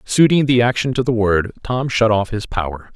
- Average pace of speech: No, fast, 225 wpm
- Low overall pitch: Yes, low, 115 Hz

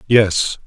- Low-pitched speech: Yes, low, 100 Hz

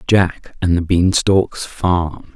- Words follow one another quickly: No, average, 155 wpm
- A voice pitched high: No, very low, 90 Hz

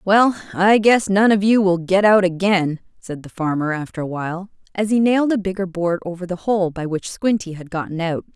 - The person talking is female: Yes, female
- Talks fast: Yes, fast, 225 wpm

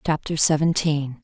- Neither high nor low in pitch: Yes, medium, 150 Hz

